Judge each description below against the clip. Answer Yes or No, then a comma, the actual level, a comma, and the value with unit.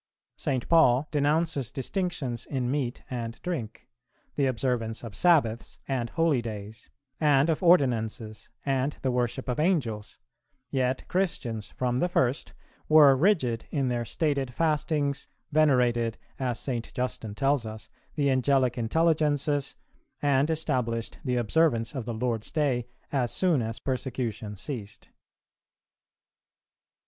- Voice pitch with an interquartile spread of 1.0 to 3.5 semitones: No, average, 3.9 semitones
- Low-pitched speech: Yes, low, 130 Hz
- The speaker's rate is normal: No, slow, 120 wpm